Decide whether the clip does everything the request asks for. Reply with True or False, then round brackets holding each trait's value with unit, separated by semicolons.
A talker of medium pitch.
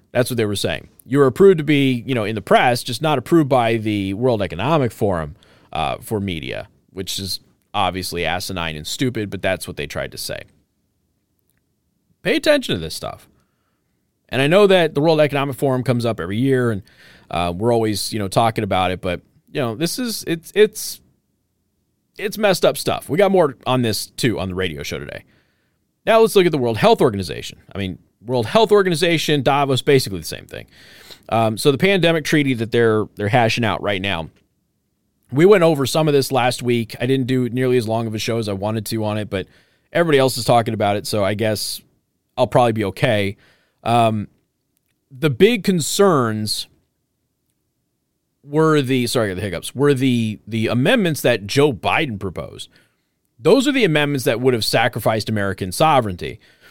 False (120 Hz)